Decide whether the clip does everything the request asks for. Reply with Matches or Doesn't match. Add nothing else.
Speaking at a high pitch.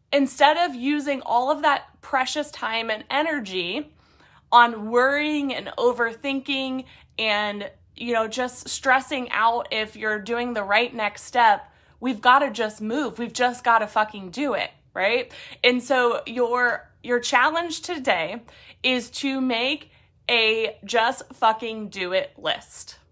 Matches